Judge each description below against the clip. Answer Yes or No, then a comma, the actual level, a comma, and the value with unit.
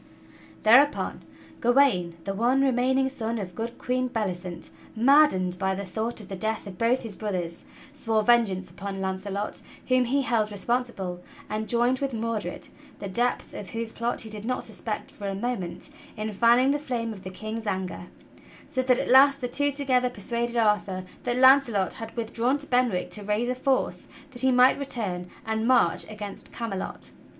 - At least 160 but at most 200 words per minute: Yes, average, 180 wpm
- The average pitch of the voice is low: No, high, 230 Hz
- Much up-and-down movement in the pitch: No, average, 4.1 semitones